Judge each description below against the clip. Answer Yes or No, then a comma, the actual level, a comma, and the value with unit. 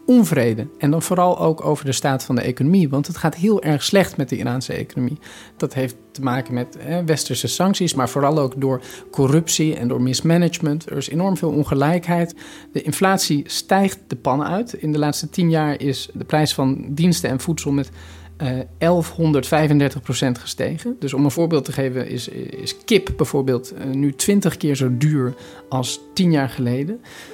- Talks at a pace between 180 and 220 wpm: Yes, average, 185 wpm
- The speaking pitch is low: No, medium, 150 Hz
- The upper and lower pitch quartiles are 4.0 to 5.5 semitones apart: Yes, average, 4.3 semitones